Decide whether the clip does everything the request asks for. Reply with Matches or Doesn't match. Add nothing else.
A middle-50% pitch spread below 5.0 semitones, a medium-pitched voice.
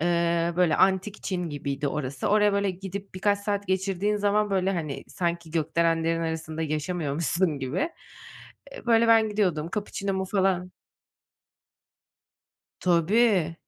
Matches